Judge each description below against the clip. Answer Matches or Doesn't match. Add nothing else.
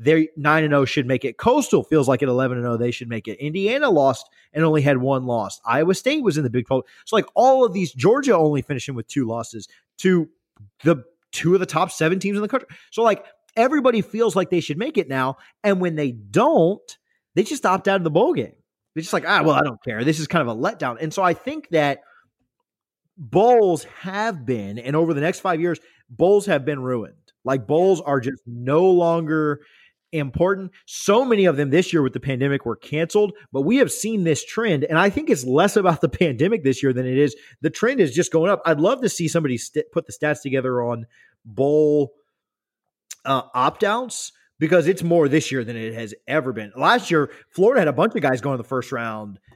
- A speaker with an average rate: Doesn't match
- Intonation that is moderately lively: Doesn't match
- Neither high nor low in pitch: Matches